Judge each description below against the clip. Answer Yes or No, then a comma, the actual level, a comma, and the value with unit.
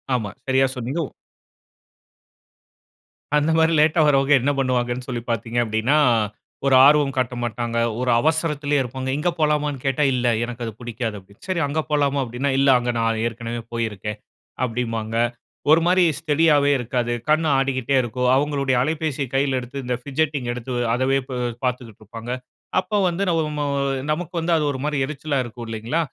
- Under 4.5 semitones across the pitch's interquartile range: Yes, average, 3.7 semitones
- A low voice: Yes, low, 130 Hz